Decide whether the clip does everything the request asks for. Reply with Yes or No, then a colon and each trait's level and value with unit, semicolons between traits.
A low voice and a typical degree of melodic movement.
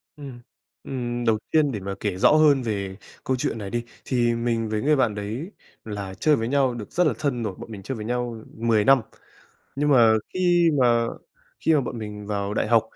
Yes: low, 120 Hz; average, 4.1 semitones